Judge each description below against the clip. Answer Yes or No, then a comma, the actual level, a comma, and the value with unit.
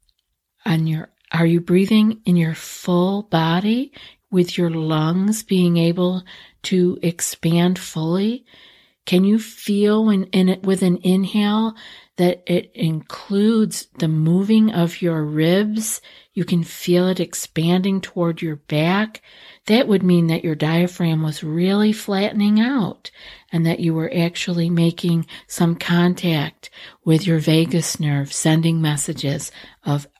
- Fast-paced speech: No, slow, 135 wpm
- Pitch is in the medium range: Yes, medium, 175 Hz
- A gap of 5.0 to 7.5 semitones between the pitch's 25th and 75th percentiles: No, average, 3.0 semitones